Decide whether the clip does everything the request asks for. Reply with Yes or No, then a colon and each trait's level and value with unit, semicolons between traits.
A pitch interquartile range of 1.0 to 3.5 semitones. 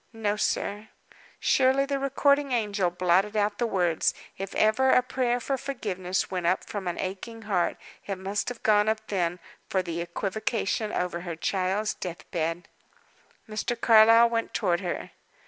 No: average, 4.0 semitones